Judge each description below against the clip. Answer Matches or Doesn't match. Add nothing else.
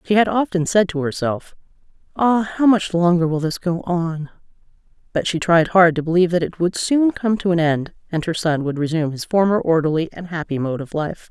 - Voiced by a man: Doesn't match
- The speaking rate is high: Matches